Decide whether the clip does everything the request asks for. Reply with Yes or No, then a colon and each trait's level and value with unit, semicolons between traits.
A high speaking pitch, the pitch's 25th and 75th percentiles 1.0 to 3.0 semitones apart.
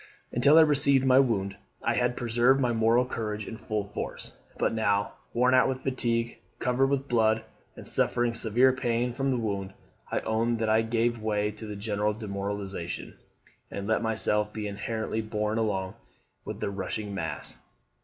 No: low, 110 Hz; average, 2.7 semitones